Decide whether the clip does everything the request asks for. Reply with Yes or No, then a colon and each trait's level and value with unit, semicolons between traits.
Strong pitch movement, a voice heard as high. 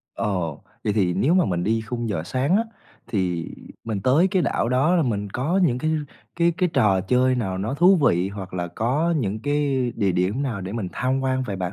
No: wide, 6.5 semitones; low, 115 Hz